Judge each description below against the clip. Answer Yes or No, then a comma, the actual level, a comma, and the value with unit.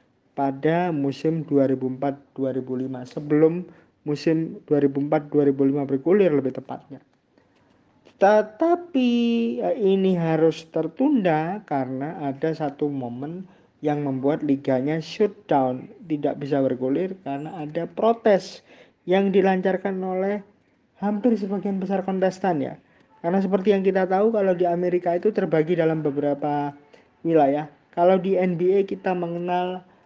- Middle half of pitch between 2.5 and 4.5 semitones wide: No, average, 4.9 semitones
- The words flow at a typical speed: Yes, average, 105 wpm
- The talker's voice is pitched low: No, medium, 165 Hz